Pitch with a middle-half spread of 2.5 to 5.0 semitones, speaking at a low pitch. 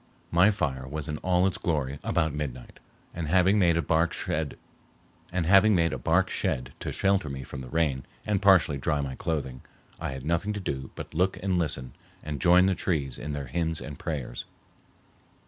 Yes: average, 4.6 semitones; very low, 80 Hz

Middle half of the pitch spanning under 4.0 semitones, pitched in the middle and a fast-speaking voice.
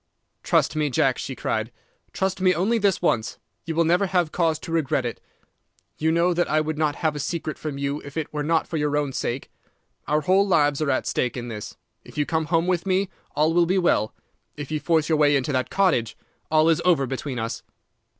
Yes: average, 3.4 semitones; medium, 155 Hz; fast, 225 wpm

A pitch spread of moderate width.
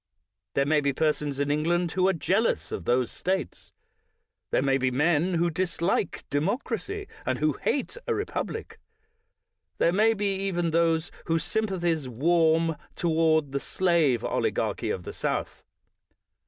Yes: average, 4.1 semitones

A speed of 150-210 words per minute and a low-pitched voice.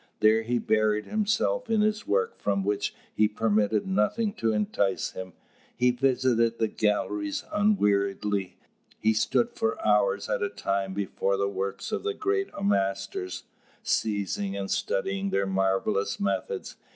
No: average, 140 wpm; low, 105 Hz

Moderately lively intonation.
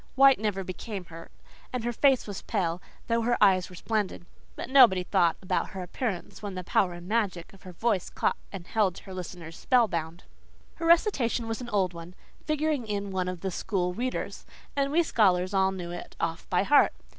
Yes: average, 4.6 semitones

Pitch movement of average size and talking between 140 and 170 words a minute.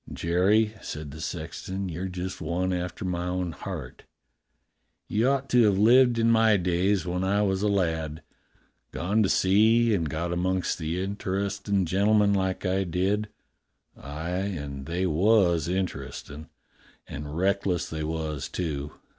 Yes: average, 3.3 semitones; average, 145 wpm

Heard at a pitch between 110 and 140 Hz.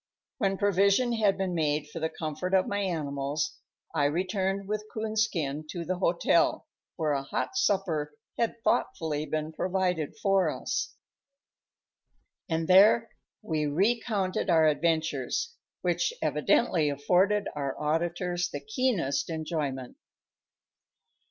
No: medium, 175 Hz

